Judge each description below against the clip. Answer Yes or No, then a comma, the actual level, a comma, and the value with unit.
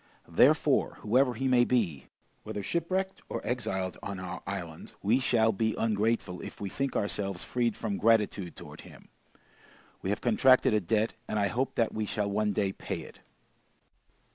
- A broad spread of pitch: No, average, 3.6 semitones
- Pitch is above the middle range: No, low, 110 Hz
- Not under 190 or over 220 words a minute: No, average, 165 wpm